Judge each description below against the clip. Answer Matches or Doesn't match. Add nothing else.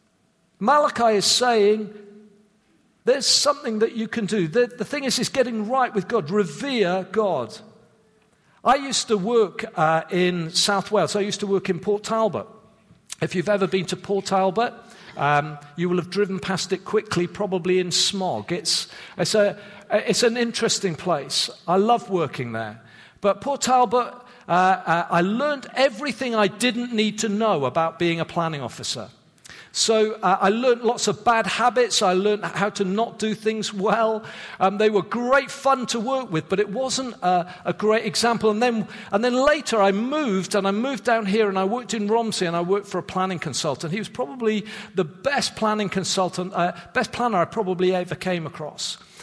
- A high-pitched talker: Matches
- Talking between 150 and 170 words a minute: Doesn't match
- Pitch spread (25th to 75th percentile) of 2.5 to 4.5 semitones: Matches